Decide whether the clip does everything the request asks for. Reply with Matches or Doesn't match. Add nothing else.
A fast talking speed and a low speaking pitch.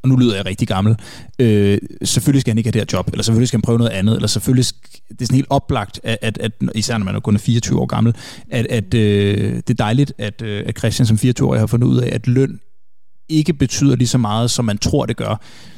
Matches